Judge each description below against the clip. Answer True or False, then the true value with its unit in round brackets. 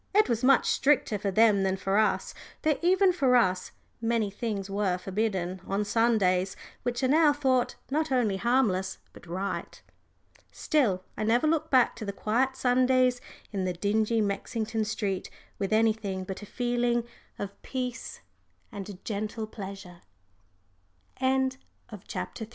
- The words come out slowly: False (145 wpm)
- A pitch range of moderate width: True (4.4 semitones)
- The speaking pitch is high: True (220 Hz)